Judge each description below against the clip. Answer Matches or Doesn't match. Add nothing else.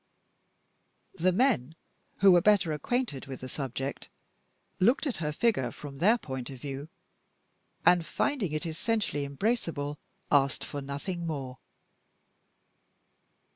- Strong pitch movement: Matches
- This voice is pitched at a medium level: Matches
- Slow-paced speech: Matches